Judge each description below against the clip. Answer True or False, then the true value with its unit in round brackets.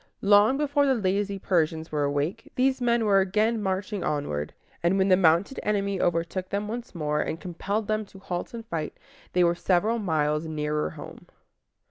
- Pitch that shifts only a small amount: False (4.7 semitones)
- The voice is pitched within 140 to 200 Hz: True (190 Hz)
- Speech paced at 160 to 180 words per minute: True (175 wpm)